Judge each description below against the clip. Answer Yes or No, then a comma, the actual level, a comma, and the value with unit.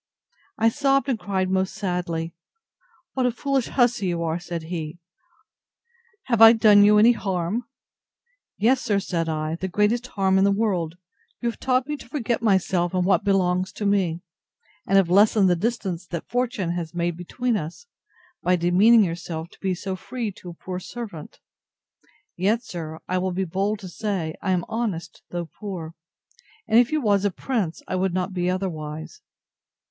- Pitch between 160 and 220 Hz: Yes, high, 190 Hz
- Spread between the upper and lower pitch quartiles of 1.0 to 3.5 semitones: No, average, 4.2 semitones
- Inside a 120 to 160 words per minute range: No, average, 175 wpm